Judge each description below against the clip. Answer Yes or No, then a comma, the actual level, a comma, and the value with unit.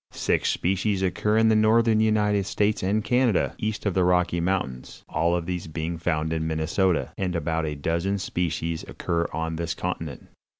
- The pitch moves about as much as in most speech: Yes, average, 4.1 semitones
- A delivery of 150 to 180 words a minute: Yes, average, 175 wpm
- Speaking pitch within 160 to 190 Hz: No, very low, 90 Hz